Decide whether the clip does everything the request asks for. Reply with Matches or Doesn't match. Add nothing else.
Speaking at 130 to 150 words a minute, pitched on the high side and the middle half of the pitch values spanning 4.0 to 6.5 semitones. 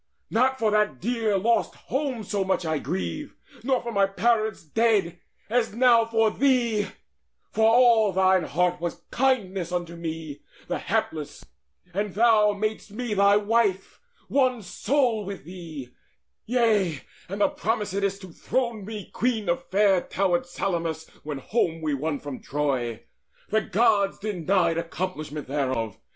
Matches